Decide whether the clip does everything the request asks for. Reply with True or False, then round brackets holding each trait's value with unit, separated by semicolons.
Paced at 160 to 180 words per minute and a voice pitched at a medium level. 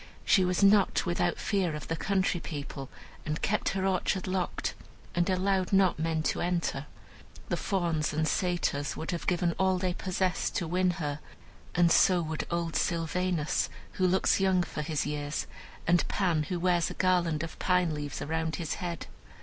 True (175 wpm; 175 Hz)